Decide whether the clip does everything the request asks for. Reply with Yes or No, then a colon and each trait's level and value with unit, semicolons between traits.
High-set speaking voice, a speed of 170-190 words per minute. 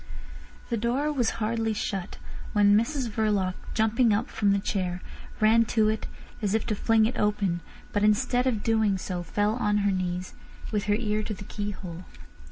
Yes: high, 210 Hz; average, 175 wpm